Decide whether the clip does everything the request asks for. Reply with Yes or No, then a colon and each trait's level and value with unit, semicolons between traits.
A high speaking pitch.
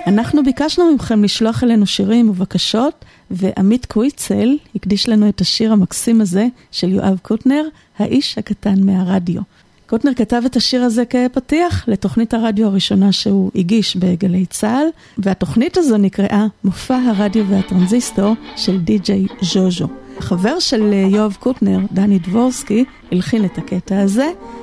Yes: high, 210 Hz